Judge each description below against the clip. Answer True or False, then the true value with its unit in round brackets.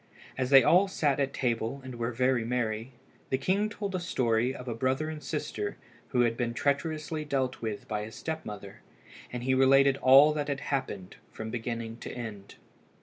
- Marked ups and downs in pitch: False (3.7 semitones)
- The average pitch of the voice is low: True (130 Hz)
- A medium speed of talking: True (190 wpm)